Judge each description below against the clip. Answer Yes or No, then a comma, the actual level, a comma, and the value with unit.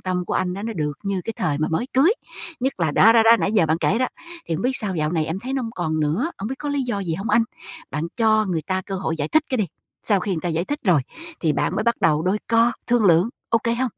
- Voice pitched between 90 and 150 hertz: No, high, 195 Hz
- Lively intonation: Yes, wide, 5.9 semitones